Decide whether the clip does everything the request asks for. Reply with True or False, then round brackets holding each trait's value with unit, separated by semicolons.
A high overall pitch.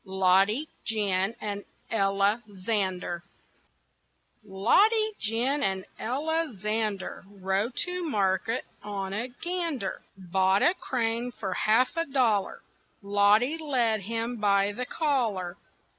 True (215 Hz)